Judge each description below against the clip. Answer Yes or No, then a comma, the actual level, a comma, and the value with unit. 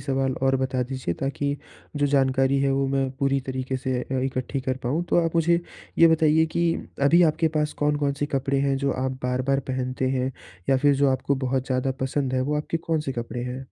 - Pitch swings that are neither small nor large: No, narrow, 1.8 semitones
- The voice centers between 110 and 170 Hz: Yes, low, 135 Hz